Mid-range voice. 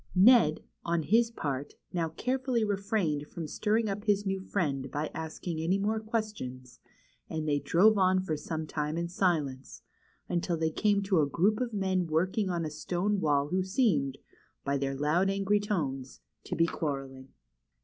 Yes: medium, 175 Hz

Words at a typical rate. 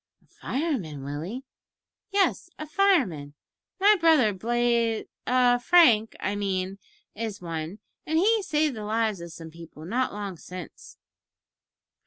No: slow, 130 wpm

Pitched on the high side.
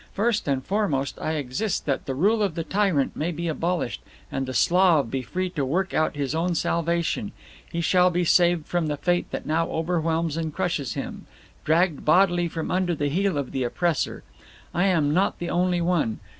No: medium, 170 Hz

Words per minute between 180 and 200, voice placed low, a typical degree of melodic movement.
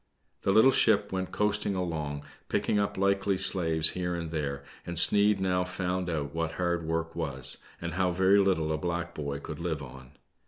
Yes: average, 185 wpm; very low, 85 Hz; average, 3.2 semitones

